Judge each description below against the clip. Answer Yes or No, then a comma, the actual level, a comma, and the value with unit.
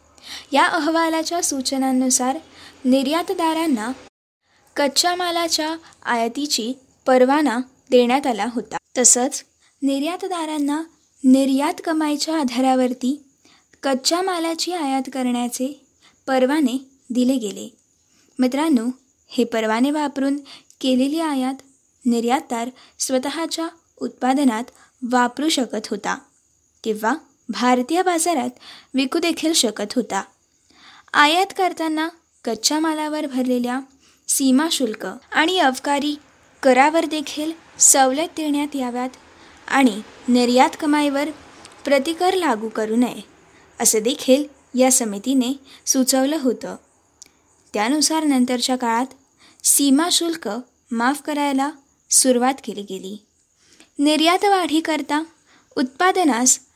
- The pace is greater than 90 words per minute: No, average, 85 wpm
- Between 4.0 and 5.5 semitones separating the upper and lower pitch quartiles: No, average, 3.6 semitones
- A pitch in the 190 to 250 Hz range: No, very high, 270 Hz